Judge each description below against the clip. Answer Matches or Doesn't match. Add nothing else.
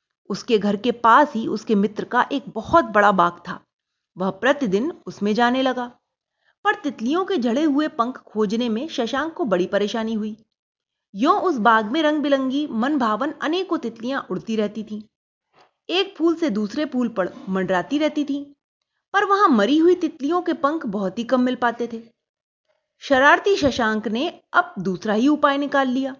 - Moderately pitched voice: Doesn't match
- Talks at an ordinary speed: Matches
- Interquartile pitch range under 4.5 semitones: Doesn't match